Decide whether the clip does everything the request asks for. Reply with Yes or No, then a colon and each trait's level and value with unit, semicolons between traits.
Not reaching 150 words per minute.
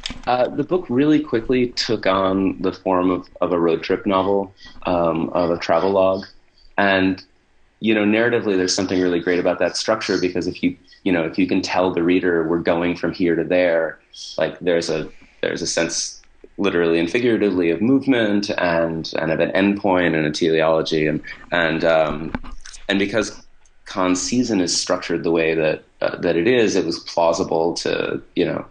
No: average, 185 wpm